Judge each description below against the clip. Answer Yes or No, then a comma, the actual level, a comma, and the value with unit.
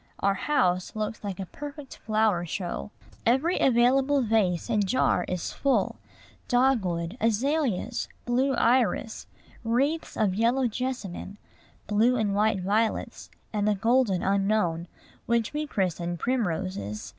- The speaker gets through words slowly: Yes, slow, 120 wpm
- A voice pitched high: Yes, high, 220 Hz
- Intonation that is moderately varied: Yes, average, 4.9 semitones